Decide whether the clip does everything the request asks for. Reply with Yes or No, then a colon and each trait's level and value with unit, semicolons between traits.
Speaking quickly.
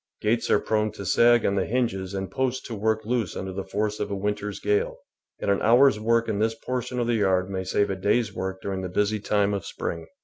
Yes: fast, 240 wpm